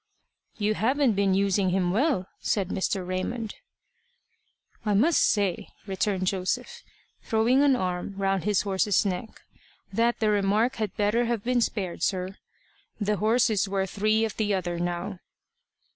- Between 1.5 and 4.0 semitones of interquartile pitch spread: Yes, average, 2.8 semitones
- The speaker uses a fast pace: No, average, 145 wpm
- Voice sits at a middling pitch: No, high, 205 Hz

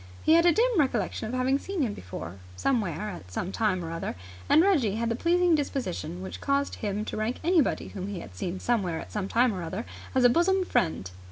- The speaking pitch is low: No, high, 225 Hz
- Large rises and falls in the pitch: Yes, wide, 7.7 semitones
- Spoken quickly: Yes, fast, 225 wpm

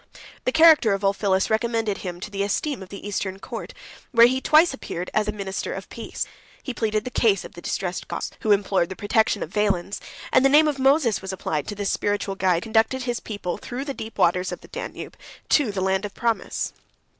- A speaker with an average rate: No, fast, 220 wpm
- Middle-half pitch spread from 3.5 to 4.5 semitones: Yes, average, 4.0 semitones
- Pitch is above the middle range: Yes, high, 210 Hz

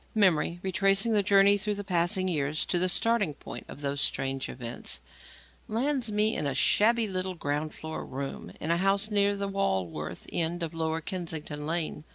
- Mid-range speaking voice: Yes, medium, 180 Hz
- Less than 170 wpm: No, average, 180 wpm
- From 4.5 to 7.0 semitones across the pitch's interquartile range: Yes, average, 4.8 semitones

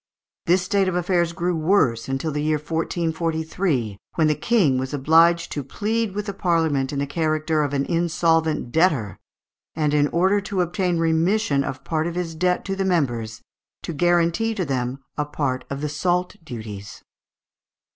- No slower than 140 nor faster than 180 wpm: Yes, average, 170 wpm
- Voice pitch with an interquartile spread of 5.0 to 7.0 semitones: No, average, 3.9 semitones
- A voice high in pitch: No, medium, 160 Hz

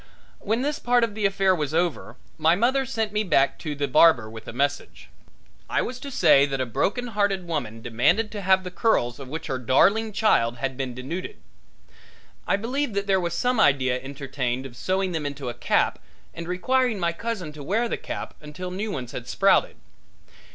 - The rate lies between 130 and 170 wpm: No, average, 200 wpm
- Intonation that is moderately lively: No, wide, 7.9 semitones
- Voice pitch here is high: No, medium, 170 Hz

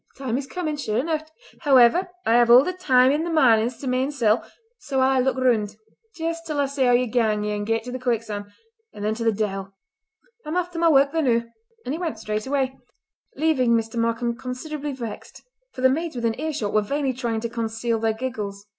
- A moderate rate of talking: No, fast, 220 wpm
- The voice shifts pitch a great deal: No, average, 4.1 semitones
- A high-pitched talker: Yes, very high, 250 Hz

